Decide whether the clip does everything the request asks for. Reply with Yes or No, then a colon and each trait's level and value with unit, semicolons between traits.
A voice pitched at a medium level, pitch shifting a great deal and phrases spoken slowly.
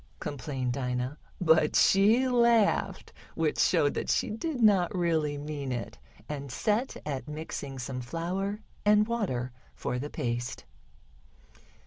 Yes: medium, 155 Hz; wide, 7.8 semitones; slow, 125 wpm